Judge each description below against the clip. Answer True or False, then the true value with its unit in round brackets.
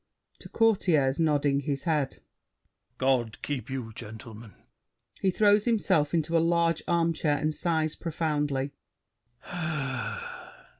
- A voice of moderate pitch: True (150 Hz)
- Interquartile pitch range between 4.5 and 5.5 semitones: False (3.8 semitones)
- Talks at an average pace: False (105 wpm)